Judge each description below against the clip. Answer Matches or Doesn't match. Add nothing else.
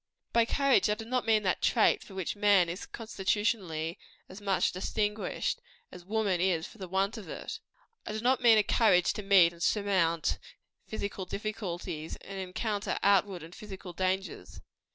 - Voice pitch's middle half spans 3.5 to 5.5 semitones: Doesn't match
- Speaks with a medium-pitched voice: Doesn't match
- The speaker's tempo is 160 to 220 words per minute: Matches